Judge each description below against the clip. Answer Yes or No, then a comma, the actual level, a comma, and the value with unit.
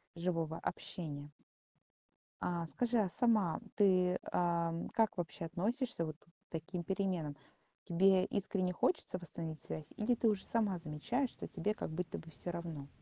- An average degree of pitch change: Yes, average, 3.6 semitones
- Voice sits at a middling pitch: Yes, medium, 180 Hz